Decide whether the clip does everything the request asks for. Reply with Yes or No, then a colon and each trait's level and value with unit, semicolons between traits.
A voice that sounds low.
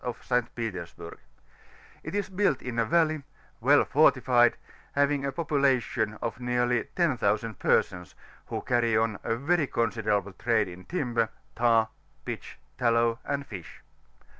Yes: low, 120 Hz